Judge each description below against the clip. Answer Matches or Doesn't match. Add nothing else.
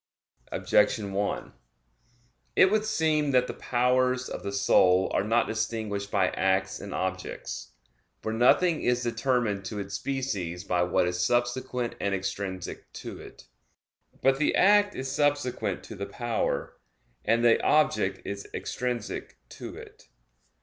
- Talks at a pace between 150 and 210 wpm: Doesn't match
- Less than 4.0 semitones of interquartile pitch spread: Doesn't match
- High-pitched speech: Doesn't match